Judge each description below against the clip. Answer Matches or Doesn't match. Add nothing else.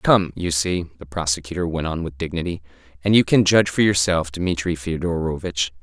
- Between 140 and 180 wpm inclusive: Matches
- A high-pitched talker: Doesn't match